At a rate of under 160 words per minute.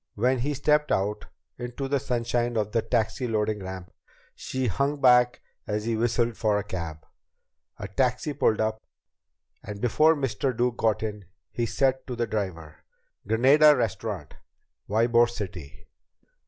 Yes: average, 145 wpm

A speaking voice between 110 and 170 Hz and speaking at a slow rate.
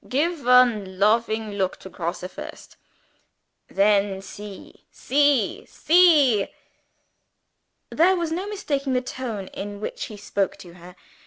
No: high, 225 Hz; slow, 125 wpm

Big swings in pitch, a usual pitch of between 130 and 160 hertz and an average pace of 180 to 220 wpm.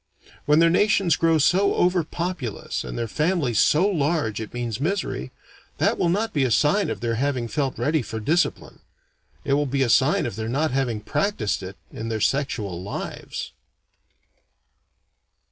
No: wide, 6.3 semitones; medium, 140 Hz; average, 165 wpm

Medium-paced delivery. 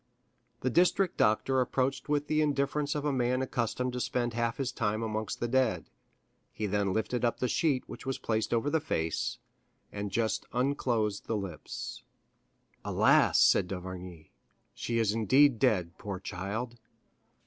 Yes: average, 150 wpm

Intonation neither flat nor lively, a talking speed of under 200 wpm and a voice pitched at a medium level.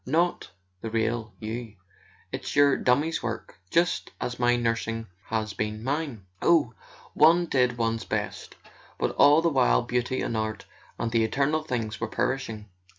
No: average, 4.3 semitones; average, 150 wpm; low, 120 Hz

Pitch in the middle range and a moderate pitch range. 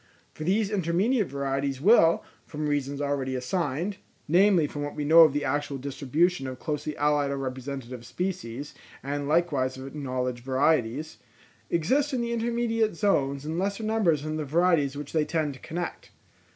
Yes: medium, 150 Hz; average, 4.4 semitones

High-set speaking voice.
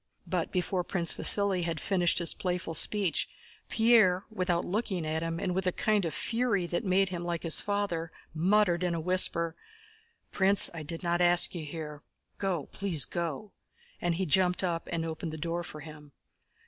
No: medium, 175 Hz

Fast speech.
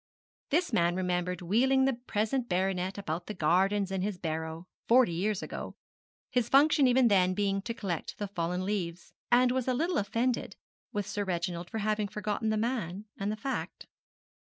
No: average, 175 wpm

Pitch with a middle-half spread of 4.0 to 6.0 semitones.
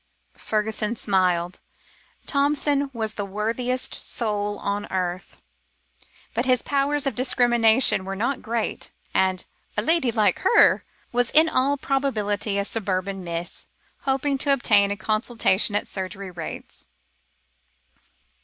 Yes: average, 4.7 semitones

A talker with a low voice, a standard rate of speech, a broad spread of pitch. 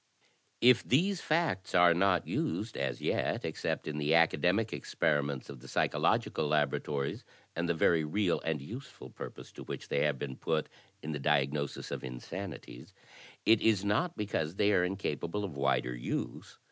Yes: very low, 85 Hz; average, 160 wpm; wide, 6.2 semitones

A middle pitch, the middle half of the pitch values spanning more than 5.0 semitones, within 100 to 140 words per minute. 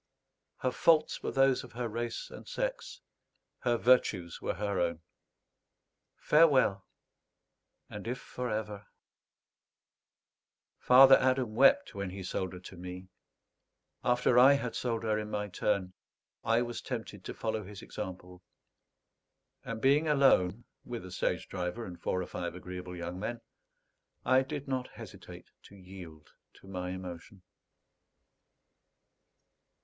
No: low, 110 Hz; wide, 5.5 semitones; slow, 135 wpm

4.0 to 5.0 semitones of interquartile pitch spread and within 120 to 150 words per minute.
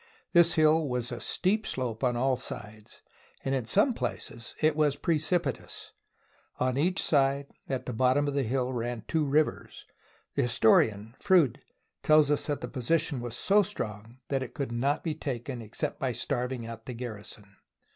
No: average, 4.4 semitones; average, 175 wpm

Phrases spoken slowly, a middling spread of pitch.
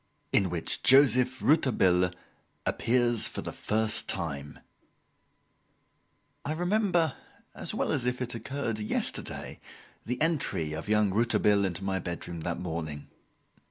No: slow, 125 wpm; wide, 6.5 semitones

